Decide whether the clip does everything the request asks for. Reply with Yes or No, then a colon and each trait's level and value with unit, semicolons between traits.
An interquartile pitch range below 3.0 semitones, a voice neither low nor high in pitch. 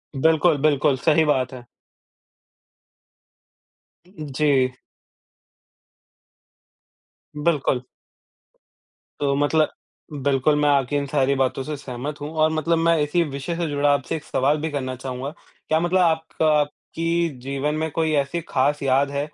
Yes: narrow, 2.5 semitones; medium, 145 Hz